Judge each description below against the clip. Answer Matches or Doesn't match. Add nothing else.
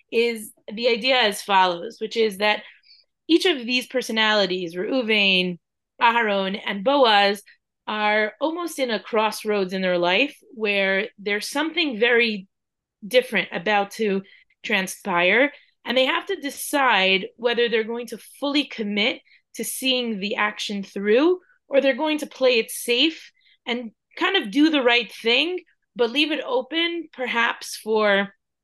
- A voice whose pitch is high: Matches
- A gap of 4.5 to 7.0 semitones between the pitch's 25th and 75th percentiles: Matches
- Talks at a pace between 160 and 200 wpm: Doesn't match